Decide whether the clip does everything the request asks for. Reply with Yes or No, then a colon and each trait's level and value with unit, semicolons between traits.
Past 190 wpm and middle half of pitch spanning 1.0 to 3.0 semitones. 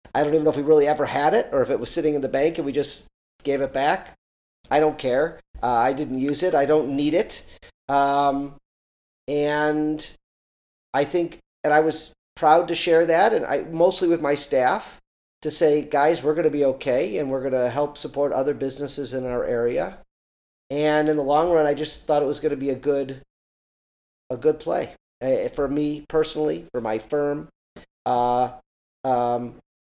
Yes: average, 200 wpm; average, 2.7 semitones